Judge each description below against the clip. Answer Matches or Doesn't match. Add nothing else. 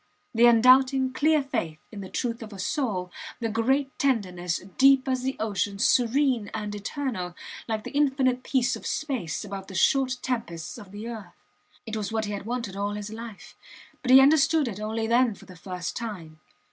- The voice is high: Matches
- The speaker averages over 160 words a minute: Matches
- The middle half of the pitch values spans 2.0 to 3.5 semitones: Doesn't match